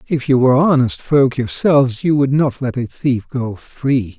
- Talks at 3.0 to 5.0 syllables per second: Yes, 4.5 syllables/s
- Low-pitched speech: Yes, low, 130 Hz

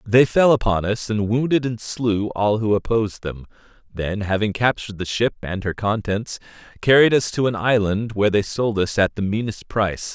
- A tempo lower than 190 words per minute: No, average, 195 wpm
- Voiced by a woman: No, male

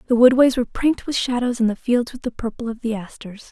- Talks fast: Yes, fast, 255 wpm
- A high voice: Yes, high, 240 Hz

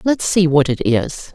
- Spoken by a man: No, female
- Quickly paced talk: Yes, fast, 220 wpm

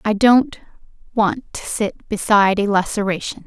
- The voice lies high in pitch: Yes, high, 210 Hz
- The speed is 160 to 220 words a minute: No, average, 140 wpm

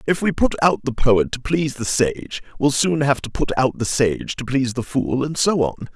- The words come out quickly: Yes, fast, 250 wpm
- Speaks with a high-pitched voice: No, low, 130 Hz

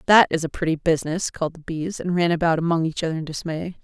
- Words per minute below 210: No, fast, 250 wpm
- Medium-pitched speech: Yes, medium, 165 Hz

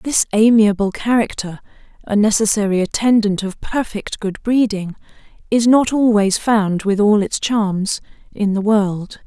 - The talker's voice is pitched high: Yes, high, 210 Hz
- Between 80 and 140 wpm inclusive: Yes, slow, 135 wpm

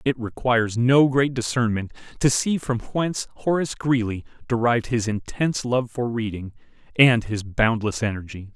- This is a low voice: Yes, low, 120 Hz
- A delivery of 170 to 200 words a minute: No, average, 145 wpm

